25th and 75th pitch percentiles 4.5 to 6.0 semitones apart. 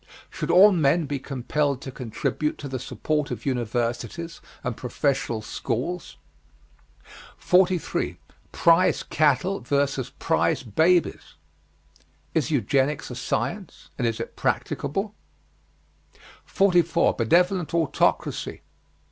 Yes: average, 5.2 semitones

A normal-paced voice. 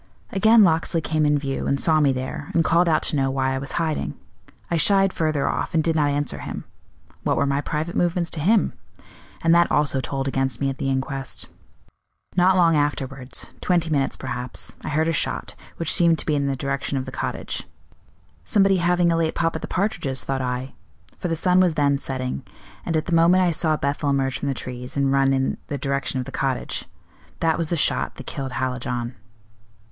No: fast, 210 wpm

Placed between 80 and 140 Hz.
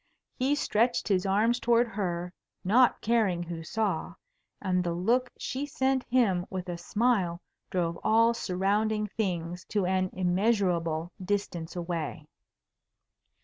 No: high, 195 Hz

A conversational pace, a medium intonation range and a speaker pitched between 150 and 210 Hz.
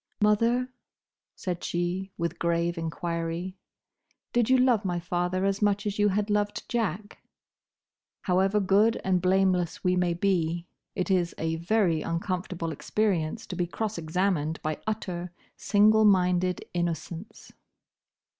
No: slow, 130 wpm; average, 3.2 semitones; medium, 185 Hz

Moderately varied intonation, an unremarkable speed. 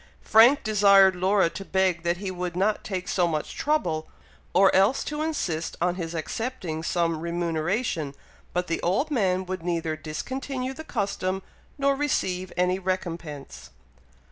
Yes: average, 3.9 semitones; average, 145 wpm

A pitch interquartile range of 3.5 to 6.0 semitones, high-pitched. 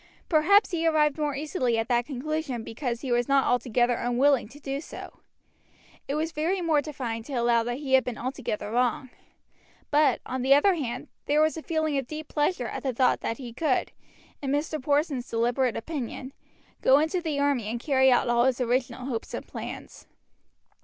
Yes: average, 3.8 semitones; very high, 270 Hz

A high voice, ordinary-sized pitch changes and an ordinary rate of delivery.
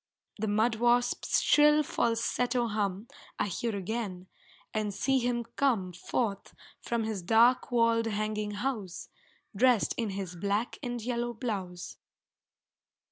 No: high, 225 Hz; average, 3.0 semitones; slow, 125 wpm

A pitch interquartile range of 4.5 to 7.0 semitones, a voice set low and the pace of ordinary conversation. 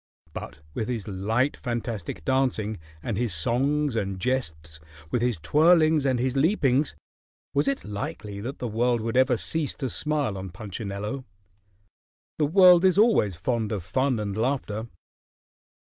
Yes: average, 5.1 semitones; low, 120 Hz; average, 145 wpm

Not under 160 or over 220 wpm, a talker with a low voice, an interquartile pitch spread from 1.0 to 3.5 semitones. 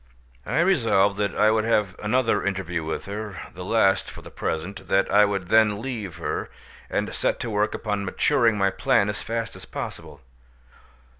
Yes: average, 165 wpm; low, 105 Hz; narrow, 2.4 semitones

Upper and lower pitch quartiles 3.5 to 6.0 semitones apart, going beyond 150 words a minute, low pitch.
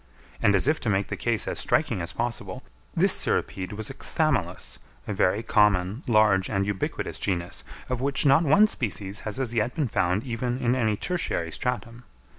Yes: average, 4.2 semitones; average, 185 wpm; low, 110 Hz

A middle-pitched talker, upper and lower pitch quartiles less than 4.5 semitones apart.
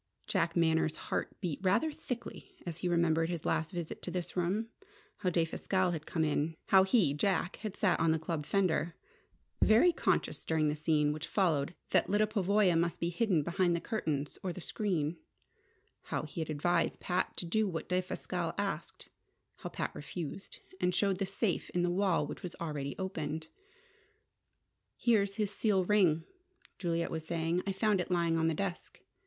Yes: medium, 175 Hz; average, 3.1 semitones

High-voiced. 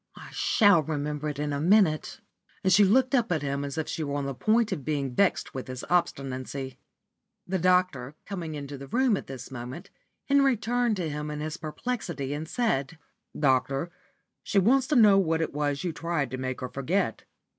No: medium, 155 Hz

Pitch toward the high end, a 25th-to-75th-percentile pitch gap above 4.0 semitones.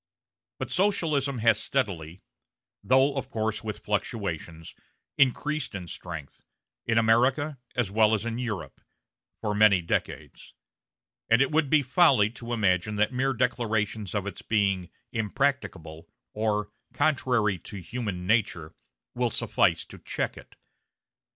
No: low, 110 Hz; average, 4.5 semitones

